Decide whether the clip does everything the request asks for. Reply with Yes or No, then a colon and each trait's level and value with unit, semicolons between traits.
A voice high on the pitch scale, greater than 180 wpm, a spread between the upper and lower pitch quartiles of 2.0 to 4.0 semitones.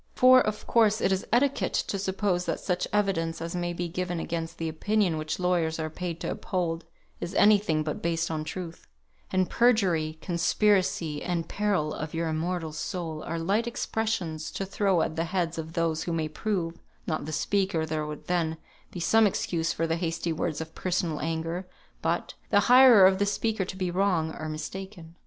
No: medium, 175 Hz; average, 190 wpm; average, 3.1 semitones